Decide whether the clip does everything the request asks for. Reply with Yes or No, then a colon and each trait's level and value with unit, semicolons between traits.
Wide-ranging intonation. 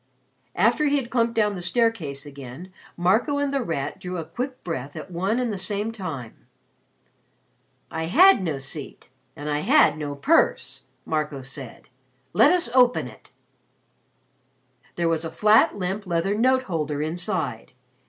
Yes: wide, 7.4 semitones